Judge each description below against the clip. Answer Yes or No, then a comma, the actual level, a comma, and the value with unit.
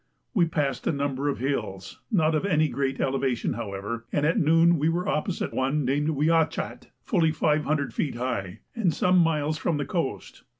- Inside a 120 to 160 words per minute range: No, average, 175 wpm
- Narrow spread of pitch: No, average, 3.5 semitones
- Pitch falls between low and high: Yes, medium, 150 Hz